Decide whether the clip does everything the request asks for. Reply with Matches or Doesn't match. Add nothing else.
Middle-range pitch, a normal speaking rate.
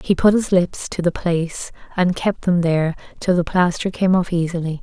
Doesn't match